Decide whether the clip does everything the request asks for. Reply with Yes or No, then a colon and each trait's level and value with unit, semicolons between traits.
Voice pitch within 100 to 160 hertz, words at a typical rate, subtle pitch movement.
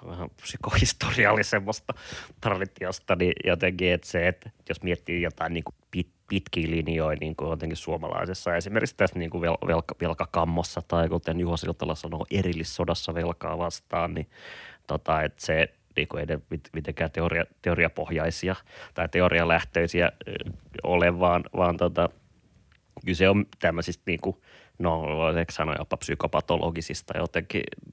No: very low, 85 Hz; average, 115 wpm; narrow, 1.3 semitones